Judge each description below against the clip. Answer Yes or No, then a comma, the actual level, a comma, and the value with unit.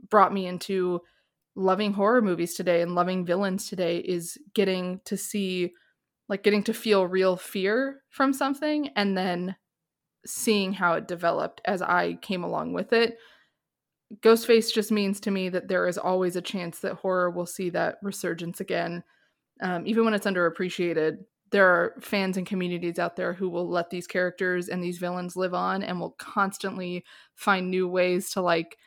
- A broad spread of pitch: No, narrow, 2.5 semitones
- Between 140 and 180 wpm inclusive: Yes, average, 175 wpm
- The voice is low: No, medium, 185 Hz